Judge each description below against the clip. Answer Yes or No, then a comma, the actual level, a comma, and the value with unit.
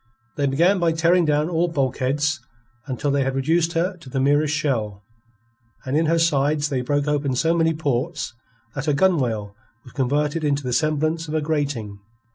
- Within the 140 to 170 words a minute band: No, average, 180 wpm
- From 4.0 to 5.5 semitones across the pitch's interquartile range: No, average, 3.2 semitones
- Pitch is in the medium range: Yes, medium, 145 Hz